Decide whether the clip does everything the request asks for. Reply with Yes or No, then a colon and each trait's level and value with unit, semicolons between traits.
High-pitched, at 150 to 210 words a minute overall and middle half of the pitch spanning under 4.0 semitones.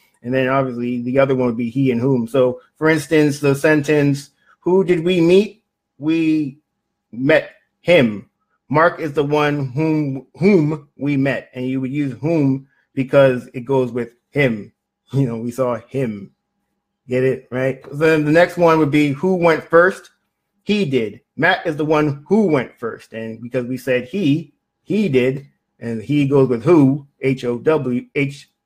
No: medium, 140 Hz; average, 175 wpm; average, 3.6 semitones